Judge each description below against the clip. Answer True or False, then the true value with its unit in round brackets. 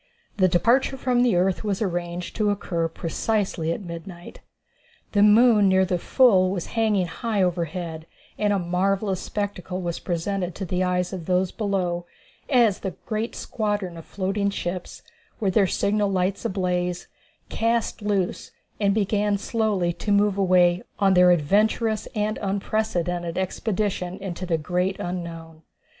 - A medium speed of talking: True (150 wpm)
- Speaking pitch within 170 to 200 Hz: True (190 Hz)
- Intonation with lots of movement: False (2.8 semitones)